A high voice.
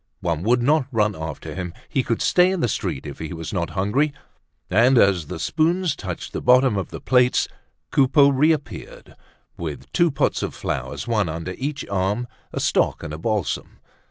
No: low, 115 Hz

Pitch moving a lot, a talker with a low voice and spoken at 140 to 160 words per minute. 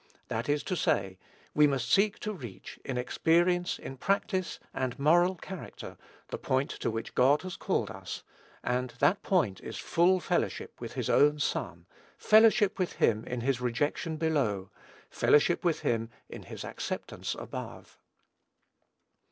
No: wide, 6.2 semitones; medium, 150 Hz; average, 150 wpm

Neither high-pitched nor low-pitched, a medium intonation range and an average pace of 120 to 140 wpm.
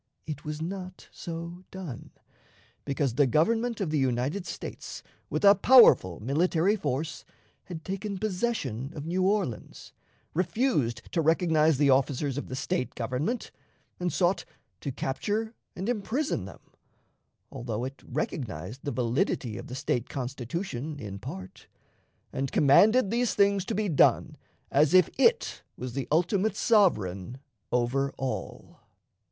No: medium, 155 Hz; wide, 6.9 semitones; slow, 135 wpm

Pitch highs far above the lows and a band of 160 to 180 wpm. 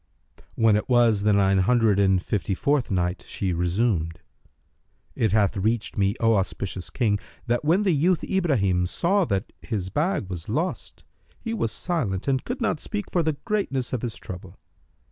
Yes: wide, 7.5 semitones; average, 170 wpm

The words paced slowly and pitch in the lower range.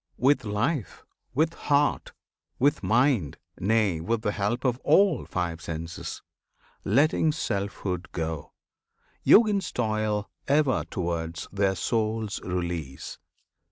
Yes: slow, 105 wpm; low, 105 Hz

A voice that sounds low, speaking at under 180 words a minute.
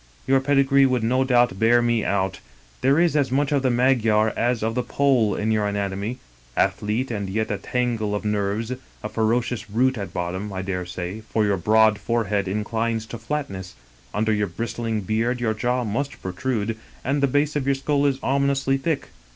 No: low, 115 Hz; average, 190 wpm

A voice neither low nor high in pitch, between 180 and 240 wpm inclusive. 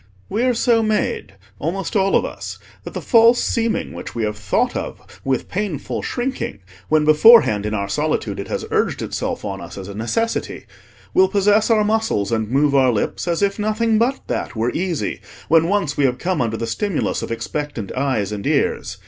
Yes: medium, 165 Hz; average, 195 wpm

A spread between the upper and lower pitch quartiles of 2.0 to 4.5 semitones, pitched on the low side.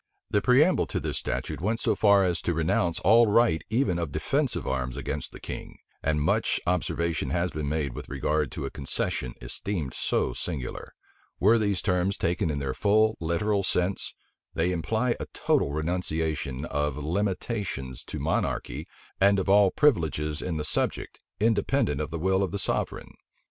No: average, 5.0 semitones; very low, 85 Hz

